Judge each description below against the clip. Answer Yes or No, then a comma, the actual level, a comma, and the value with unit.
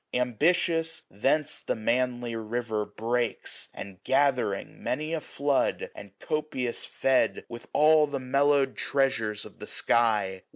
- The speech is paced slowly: Yes, slow, 125 wpm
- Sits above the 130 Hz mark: No, low, 125 Hz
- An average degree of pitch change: Yes, average, 4.2 semitones